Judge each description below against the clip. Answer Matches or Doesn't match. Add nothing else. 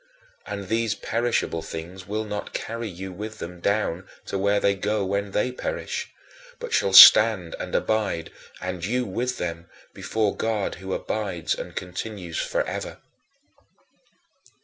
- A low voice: Matches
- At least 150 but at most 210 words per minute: Doesn't match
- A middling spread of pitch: Matches